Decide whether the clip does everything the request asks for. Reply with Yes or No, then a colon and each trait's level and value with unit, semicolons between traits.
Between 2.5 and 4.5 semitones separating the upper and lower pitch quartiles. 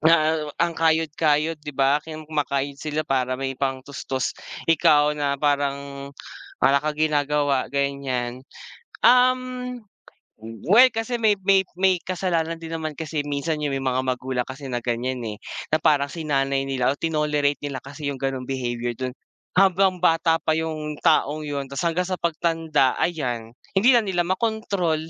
Yes: average, 3.3 semitones